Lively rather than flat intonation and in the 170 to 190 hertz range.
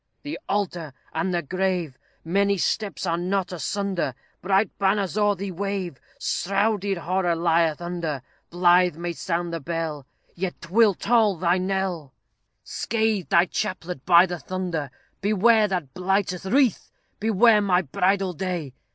No: average, 2.7 semitones; medium, 185 Hz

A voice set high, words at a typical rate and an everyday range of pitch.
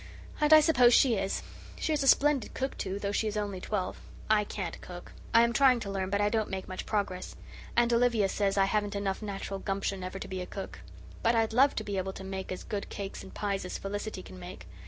No: high, 205 Hz; fast, 240 wpm; average, 3.1 semitones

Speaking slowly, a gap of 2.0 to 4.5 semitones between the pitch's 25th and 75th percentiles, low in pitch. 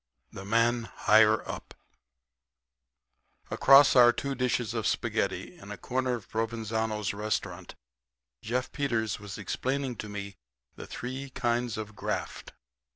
Yes: slow, 130 wpm; average, 2.8 semitones; low, 115 Hz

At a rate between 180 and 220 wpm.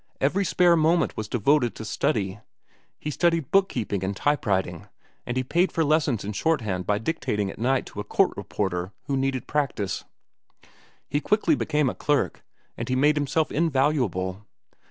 No: average, 170 wpm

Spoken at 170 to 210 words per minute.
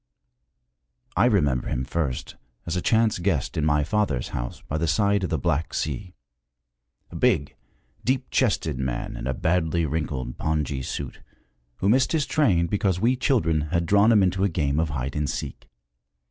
Yes: average, 175 wpm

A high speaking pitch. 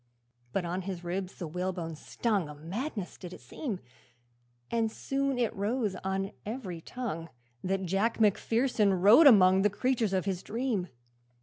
Yes: high, 195 Hz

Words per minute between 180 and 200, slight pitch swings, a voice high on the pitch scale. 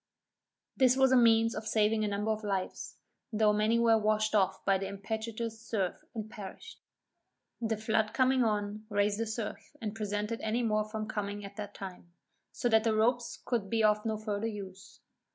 Yes: average, 185 wpm; narrow, 1.6 semitones; high, 215 Hz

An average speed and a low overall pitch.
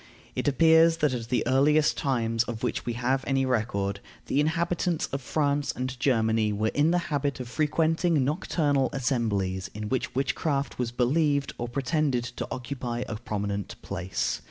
Yes: average, 160 wpm; low, 130 Hz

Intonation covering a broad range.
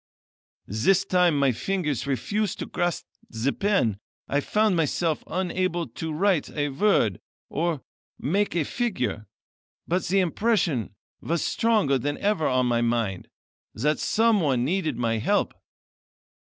Yes: wide, 7.1 semitones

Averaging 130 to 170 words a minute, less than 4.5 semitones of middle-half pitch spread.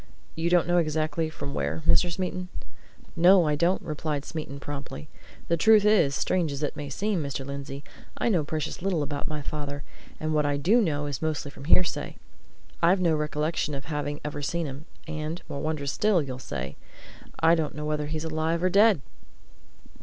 No: average, 185 wpm; average, 2.9 semitones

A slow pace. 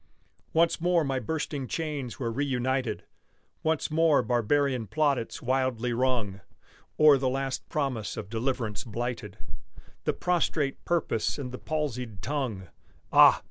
Yes: slow, 125 wpm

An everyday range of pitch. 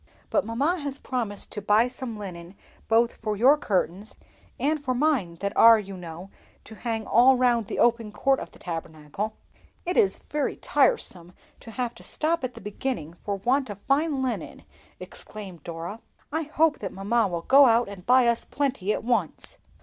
Yes: average, 5.0 semitones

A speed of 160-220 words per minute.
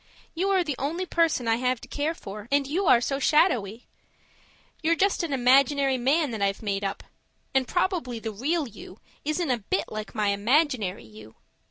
Yes: average, 185 wpm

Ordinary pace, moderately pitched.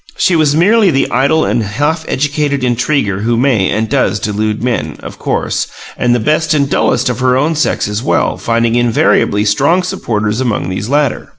No: average, 185 wpm; low, 125 Hz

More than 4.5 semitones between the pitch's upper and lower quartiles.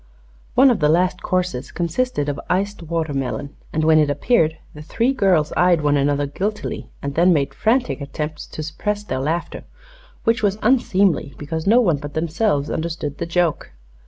Yes: average, 5.1 semitones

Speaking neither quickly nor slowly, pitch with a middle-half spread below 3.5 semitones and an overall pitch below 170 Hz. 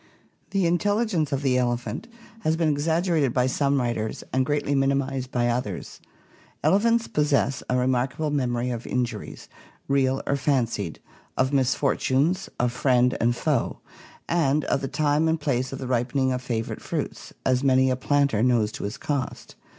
Yes: average, 160 wpm; average, 2.9 semitones; low, 135 Hz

